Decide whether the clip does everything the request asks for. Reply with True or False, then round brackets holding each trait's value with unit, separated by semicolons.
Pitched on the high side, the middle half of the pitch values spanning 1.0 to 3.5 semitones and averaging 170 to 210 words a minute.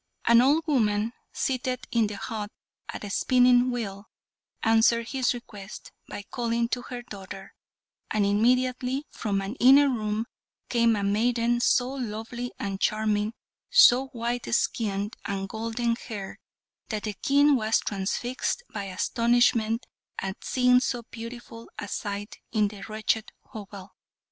False (230 Hz; 2.9 semitones; 135 wpm)